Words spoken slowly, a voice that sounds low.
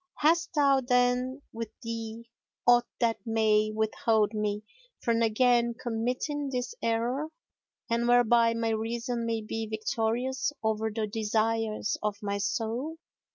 No: slow, 125 wpm; high, 230 Hz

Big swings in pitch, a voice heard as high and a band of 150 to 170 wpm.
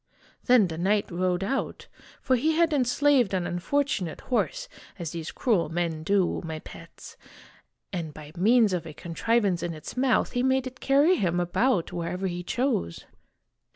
Yes: wide, 7.0 semitones; high, 195 Hz; average, 160 wpm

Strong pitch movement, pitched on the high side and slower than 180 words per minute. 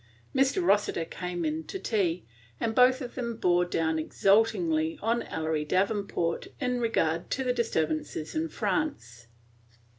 Yes: wide, 7.4 semitones; high, 205 Hz; average, 140 wpm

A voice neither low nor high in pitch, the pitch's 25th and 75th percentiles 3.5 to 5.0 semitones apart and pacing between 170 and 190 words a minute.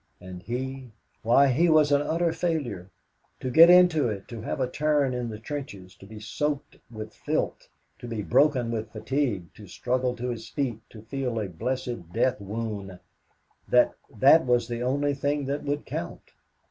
No: low, 125 Hz; average, 4.6 semitones; average, 175 wpm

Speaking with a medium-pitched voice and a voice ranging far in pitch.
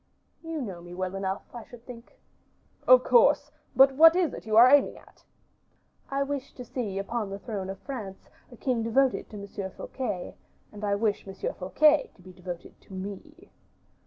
No: high, 225 Hz; wide, 5.7 semitones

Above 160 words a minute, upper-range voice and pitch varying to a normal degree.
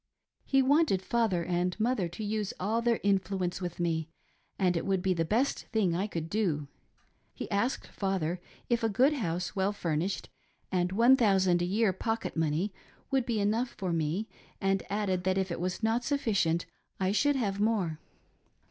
Yes: average, 175 wpm; high, 195 Hz; average, 4.0 semitones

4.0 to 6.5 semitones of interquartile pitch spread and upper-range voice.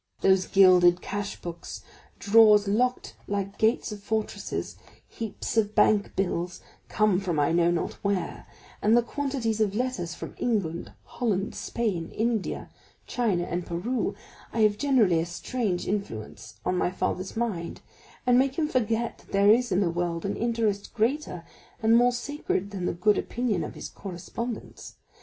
Yes: average, 4.5 semitones; high, 205 Hz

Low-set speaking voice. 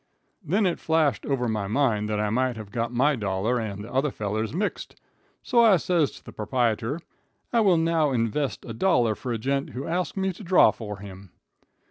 Yes: low, 125 Hz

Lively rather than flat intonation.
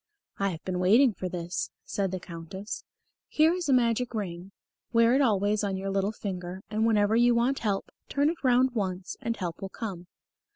No: average, 4.1 semitones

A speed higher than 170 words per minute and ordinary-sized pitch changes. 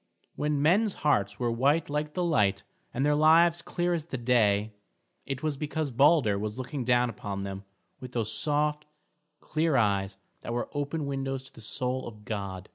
No: average, 180 wpm; wide, 5.7 semitones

